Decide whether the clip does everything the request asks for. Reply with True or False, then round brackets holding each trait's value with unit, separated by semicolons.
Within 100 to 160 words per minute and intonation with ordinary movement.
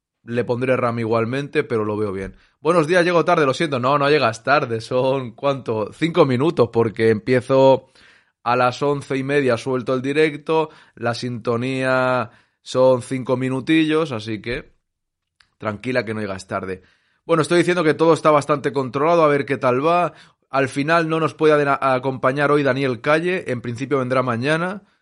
False (170 wpm; 4.0 semitones)